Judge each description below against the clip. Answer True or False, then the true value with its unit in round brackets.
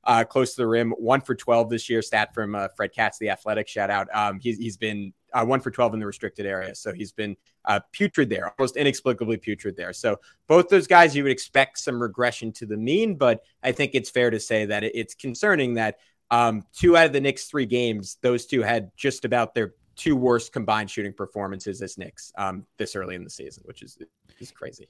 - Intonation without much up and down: False (3.5 semitones)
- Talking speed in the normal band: False (230 wpm)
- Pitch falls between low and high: False (115 Hz)